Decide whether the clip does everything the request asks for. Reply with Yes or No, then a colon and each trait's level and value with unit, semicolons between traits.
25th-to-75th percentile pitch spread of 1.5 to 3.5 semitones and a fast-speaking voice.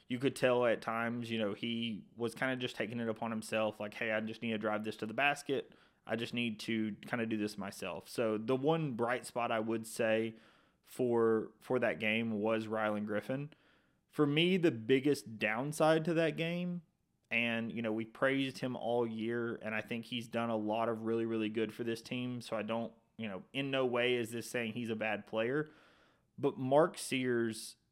Yes: narrow, 2.4 semitones; fast, 215 wpm